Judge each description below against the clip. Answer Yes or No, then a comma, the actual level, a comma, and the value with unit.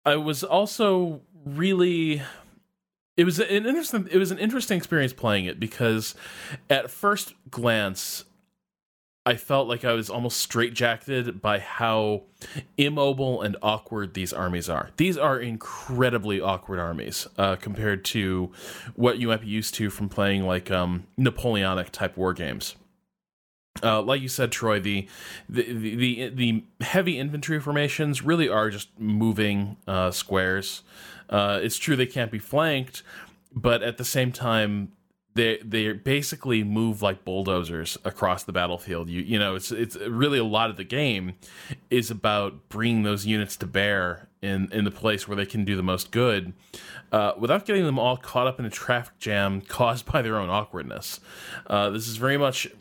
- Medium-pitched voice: No, low, 115 Hz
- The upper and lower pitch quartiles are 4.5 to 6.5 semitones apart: Yes, average, 5.0 semitones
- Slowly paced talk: No, average, 165 wpm